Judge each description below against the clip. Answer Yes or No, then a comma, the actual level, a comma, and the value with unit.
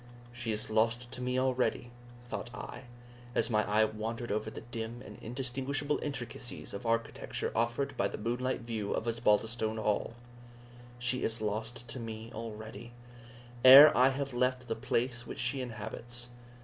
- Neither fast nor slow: Yes, average, 155 wpm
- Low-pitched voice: Yes, low, 120 Hz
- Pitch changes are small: Yes, narrow, 2.3 semitones